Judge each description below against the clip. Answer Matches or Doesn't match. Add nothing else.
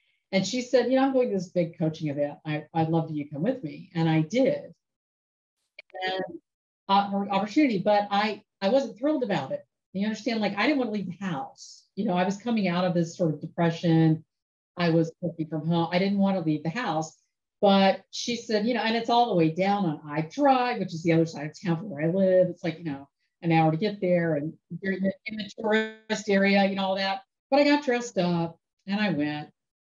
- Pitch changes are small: Doesn't match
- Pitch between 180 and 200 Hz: Matches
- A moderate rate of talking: Doesn't match